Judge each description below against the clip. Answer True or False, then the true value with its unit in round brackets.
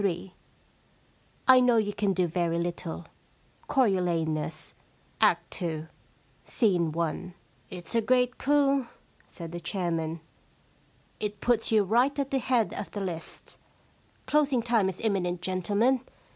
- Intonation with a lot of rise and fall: True (6.0 semitones)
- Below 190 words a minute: True (135 wpm)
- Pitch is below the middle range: False (195 Hz)